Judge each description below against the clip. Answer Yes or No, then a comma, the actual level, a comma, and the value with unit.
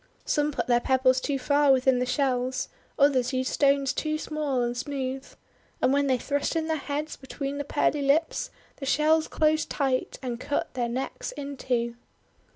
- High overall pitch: Yes, very high, 275 Hz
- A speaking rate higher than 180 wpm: No, average, 175 wpm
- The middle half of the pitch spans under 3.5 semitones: Yes, narrow, 2.4 semitones